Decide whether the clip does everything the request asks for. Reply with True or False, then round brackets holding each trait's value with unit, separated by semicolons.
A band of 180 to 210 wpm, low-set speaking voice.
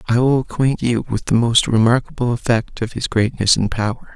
True (200 wpm; 120 Hz)